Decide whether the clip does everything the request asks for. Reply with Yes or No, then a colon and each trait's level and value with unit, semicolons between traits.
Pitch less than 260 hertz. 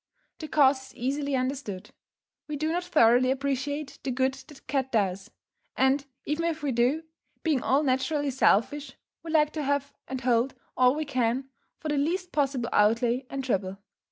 No: very high, 270 Hz